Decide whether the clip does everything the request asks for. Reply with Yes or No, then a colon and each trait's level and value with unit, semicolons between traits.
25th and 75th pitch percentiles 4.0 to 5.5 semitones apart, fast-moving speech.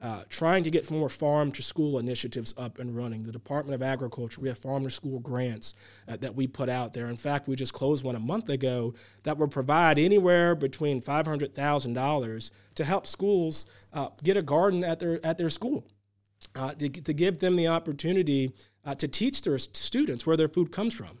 No: average, 4.6 semitones; average, 190 wpm